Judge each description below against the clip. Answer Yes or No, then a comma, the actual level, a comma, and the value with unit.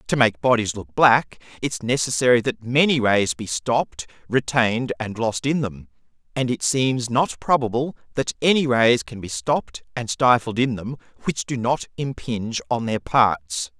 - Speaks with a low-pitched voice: Yes, low, 120 Hz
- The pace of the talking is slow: No, average, 170 wpm